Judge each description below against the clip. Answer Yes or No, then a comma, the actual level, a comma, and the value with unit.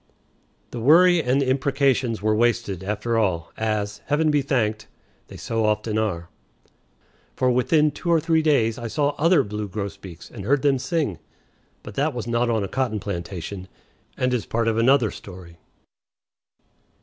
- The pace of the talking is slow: No, average, 160 wpm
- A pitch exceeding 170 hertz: No, low, 115 Hz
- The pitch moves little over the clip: No, average, 4.8 semitones